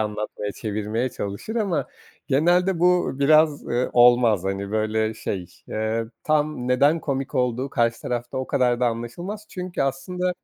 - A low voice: Yes, low, 125 Hz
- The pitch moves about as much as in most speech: No, wide, 5.9 semitones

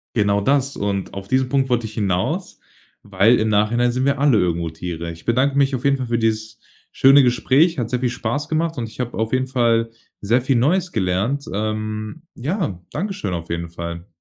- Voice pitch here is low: Yes, low, 115 Hz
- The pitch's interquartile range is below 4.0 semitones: No, average, 4.9 semitones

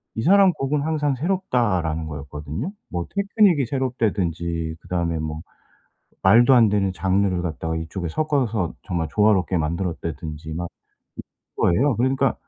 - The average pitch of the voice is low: Yes, very low, 95 Hz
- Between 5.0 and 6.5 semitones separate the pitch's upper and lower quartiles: No, wide, 8.2 semitones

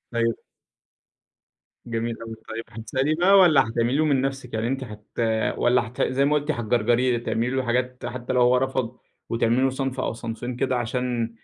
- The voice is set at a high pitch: No, low, 125 Hz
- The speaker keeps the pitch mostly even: Yes, narrow, 2.3 semitones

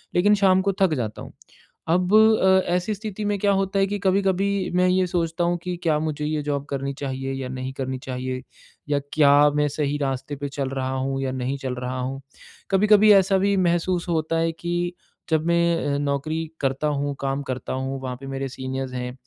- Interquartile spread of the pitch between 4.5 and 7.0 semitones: Yes, average, 5.3 semitones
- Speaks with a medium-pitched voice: Yes, medium, 150 Hz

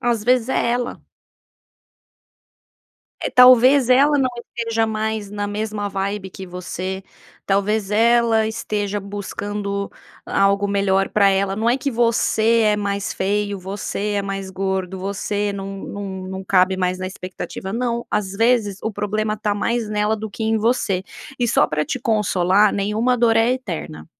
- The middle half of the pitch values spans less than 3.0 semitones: Yes, narrow, 2.5 semitones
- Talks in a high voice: Yes, high, 205 Hz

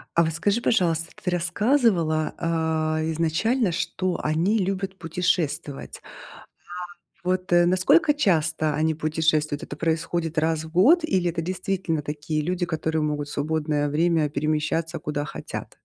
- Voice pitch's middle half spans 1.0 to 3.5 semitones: Yes, average, 3.0 semitones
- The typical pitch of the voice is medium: Yes, medium, 165 Hz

